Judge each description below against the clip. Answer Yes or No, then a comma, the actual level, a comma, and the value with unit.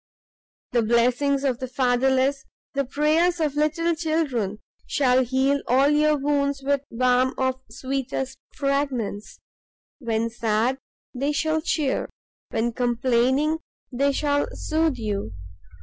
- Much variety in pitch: No, average, 2.9 semitones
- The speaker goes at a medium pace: No, slow, 120 wpm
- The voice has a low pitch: No, very high, 270 Hz